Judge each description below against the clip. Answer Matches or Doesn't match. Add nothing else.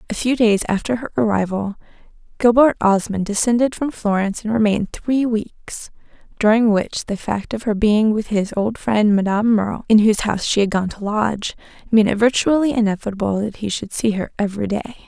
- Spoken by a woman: Matches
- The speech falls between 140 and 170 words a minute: Doesn't match